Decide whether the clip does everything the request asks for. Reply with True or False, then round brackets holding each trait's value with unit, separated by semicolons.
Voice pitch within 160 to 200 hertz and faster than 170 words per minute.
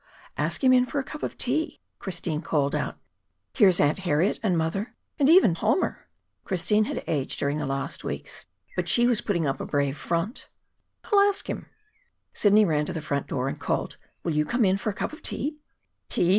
True (190 Hz; 200 wpm)